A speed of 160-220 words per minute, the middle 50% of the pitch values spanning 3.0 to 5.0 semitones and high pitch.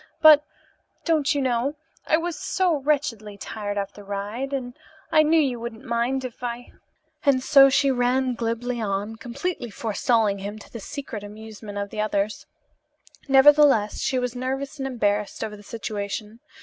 Yes: average, 165 wpm; average, 4.5 semitones; high, 240 Hz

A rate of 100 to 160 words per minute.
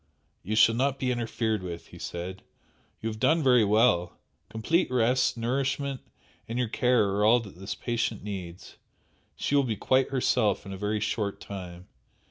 No: average, 170 wpm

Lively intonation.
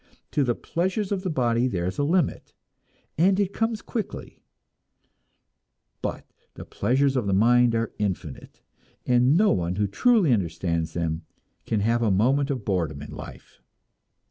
Yes: wide, 8.6 semitones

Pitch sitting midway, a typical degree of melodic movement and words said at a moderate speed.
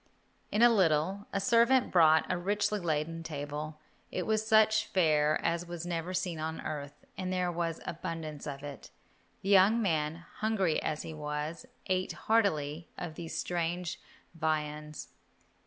Yes: medium, 170 Hz; average, 3.7 semitones; average, 150 wpm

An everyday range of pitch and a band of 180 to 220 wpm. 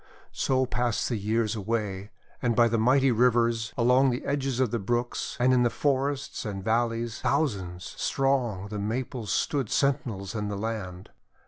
No: average, 3.4 semitones; average, 160 wpm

